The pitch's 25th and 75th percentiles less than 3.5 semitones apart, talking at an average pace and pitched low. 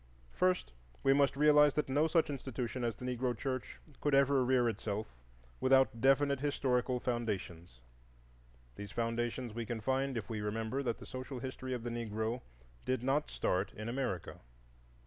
Yes: average, 3.1 semitones; average, 155 wpm; low, 125 Hz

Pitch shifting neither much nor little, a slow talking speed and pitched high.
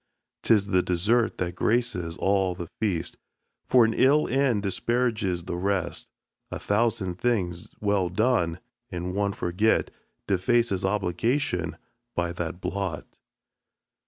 No: average, 4.4 semitones; slow, 120 wpm; low, 100 Hz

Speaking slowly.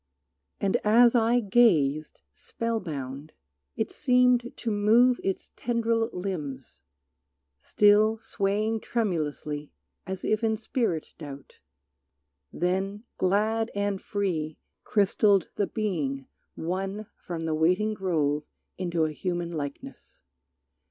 Yes: slow, 105 wpm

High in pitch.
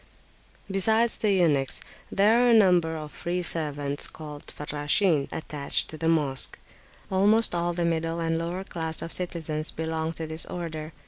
No: medium, 165 Hz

